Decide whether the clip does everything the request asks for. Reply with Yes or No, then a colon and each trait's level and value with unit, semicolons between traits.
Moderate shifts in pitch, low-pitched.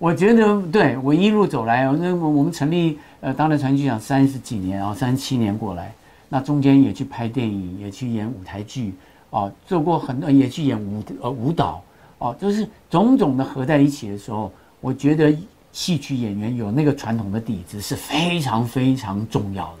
No: wide, 6.1 semitones; low, 130 Hz